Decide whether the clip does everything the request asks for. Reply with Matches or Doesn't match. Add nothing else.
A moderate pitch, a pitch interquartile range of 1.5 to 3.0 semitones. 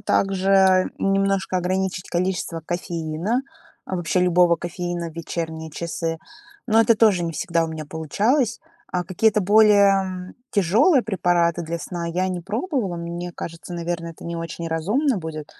Matches